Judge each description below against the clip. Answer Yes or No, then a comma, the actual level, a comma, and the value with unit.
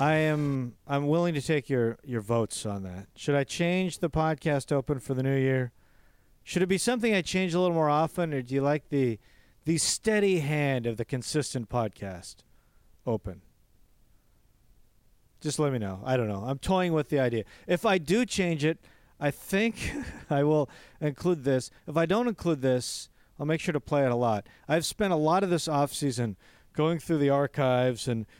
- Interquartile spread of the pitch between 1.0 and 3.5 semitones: No, average, 5.1 semitones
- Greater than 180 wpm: Yes, average, 195 wpm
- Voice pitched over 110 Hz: Yes, medium, 140 Hz